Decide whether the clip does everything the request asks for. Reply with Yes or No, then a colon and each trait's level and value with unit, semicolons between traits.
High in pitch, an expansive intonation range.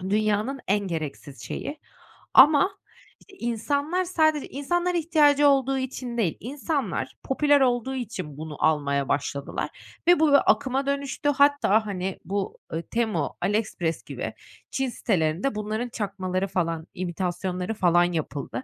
Yes: high, 220 Hz; wide, 8.0 semitones